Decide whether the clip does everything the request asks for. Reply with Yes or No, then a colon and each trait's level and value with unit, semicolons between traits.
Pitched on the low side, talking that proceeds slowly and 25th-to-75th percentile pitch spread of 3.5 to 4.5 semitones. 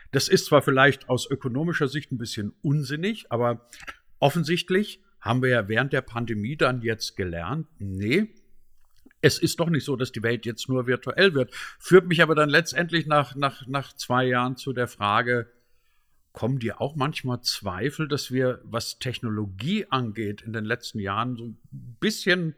No: low, 130 Hz; average, 170 wpm; average, 4.2 semitones